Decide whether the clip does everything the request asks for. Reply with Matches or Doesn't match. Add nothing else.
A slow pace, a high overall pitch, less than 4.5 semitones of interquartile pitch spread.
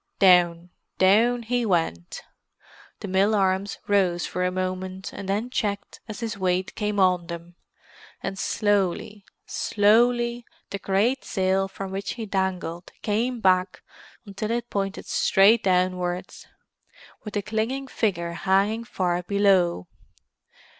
Matches